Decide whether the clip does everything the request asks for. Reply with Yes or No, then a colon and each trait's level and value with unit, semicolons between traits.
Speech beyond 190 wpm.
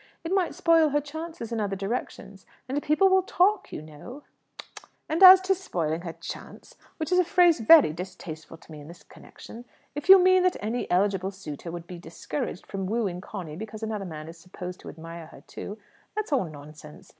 Yes: average, 200 wpm